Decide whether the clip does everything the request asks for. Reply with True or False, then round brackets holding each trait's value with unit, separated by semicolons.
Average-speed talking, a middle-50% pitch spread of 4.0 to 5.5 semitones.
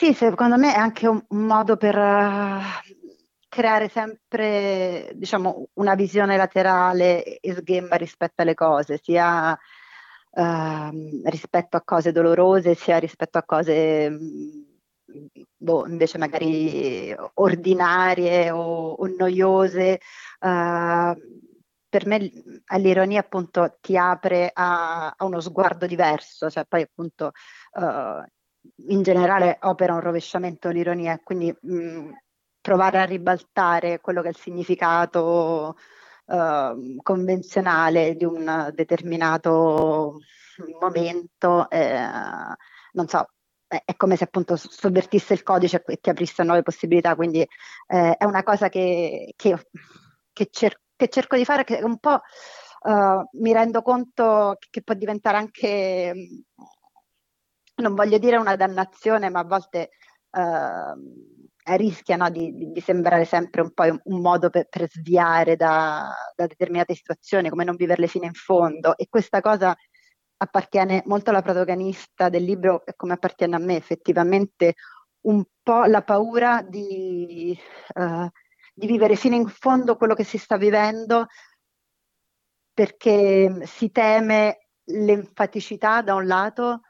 False (130 wpm; 3.4 semitones)